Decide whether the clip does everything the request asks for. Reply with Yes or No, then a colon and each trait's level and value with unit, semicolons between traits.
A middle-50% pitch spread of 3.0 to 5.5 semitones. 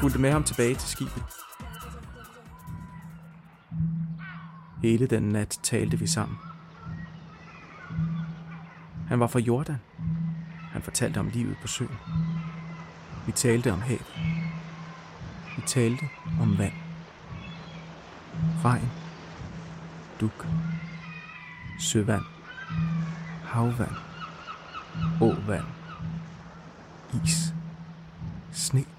Yes: average, 3.7 semitones